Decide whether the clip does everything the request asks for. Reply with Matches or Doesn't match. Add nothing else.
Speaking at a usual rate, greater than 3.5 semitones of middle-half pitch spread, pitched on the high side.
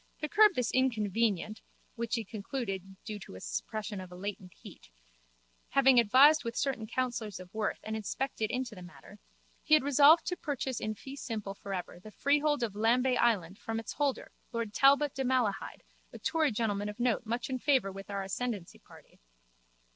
Matches